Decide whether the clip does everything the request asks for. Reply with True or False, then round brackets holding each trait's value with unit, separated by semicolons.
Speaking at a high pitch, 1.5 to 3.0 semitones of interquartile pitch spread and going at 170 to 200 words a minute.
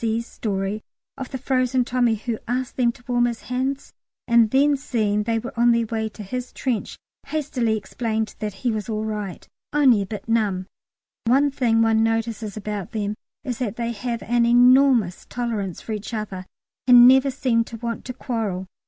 True (230 Hz; 2.6 semitones; 185 wpm)